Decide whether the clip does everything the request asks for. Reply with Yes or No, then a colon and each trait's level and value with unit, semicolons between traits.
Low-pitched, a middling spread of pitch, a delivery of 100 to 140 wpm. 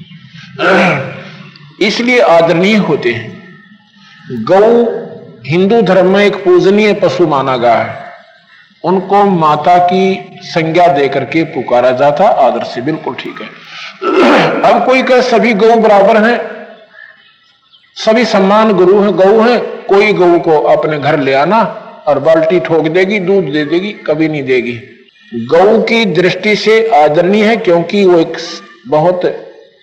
No: high, 190 Hz; average, 4.6 semitones; average, 135 wpm